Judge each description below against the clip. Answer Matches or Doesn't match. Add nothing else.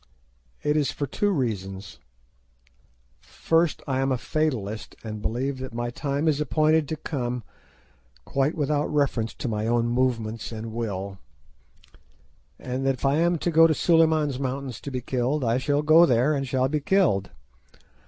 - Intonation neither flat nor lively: Matches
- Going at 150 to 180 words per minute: Matches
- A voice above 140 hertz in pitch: Doesn't match